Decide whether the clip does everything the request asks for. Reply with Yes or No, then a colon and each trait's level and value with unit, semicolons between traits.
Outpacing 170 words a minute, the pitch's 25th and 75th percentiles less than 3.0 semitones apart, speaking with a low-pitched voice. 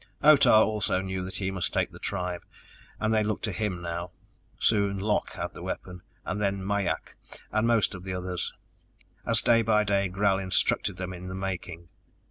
Yes: average, 185 wpm; narrow, 2.5 semitones; very low, 95 Hz